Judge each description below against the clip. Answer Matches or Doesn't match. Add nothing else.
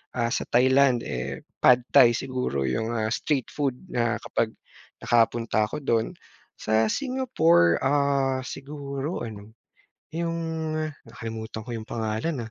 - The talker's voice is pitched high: Doesn't match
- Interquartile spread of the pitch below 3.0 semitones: Doesn't match